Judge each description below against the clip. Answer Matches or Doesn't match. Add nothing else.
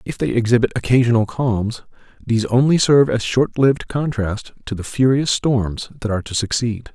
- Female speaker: Doesn't match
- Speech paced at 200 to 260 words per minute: Doesn't match